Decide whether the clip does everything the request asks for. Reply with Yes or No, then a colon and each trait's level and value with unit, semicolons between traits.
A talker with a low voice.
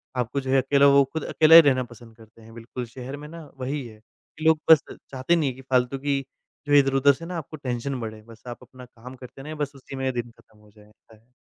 Yes: low, 130 Hz